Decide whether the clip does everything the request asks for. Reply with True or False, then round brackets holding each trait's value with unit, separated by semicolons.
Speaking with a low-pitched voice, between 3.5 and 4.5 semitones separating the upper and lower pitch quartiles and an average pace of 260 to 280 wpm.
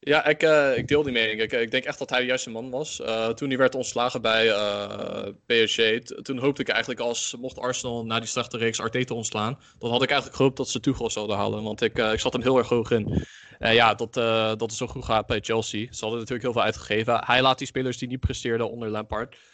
False (120 Hz; 2.6 semitones; 265 wpm)